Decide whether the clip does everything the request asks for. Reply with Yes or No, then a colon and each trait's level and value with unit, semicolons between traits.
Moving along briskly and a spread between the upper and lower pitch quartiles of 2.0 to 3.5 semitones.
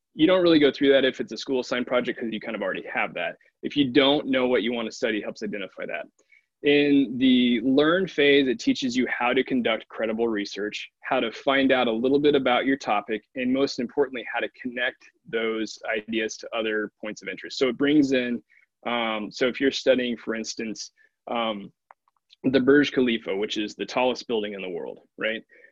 No: fast, 210 wpm; average, 4.0 semitones